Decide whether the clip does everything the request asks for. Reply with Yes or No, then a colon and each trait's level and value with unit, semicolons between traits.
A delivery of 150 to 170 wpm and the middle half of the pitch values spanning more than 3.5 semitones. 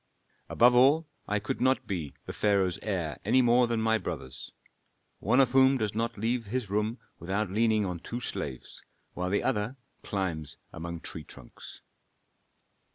Yes: average, 160 wpm; average, 4.9 semitones